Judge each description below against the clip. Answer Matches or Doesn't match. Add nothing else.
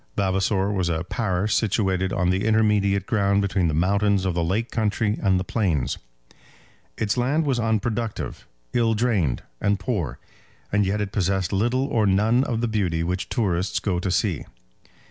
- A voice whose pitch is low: Matches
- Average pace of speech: Matches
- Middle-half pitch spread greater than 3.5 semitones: Doesn't match